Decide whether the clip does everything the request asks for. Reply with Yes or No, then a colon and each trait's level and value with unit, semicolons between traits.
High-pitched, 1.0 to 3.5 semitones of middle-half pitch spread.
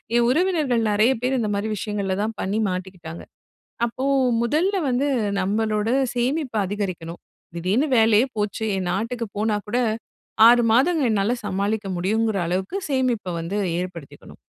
No: high, 215 Hz; average, 4.0 semitones